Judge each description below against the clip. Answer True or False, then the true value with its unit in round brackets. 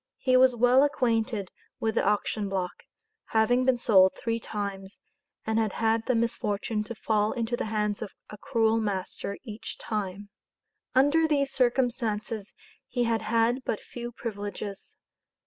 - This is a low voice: False (225 Hz)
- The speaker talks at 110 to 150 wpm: True (145 wpm)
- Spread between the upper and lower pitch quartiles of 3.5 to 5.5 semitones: False (2.8 semitones)